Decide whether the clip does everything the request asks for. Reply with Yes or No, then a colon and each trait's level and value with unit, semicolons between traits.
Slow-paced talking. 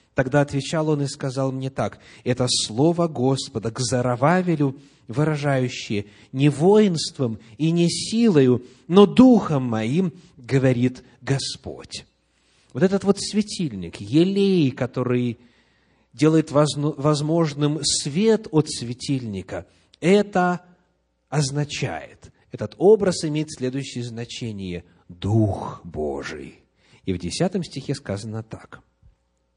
Yes: slow, 100 wpm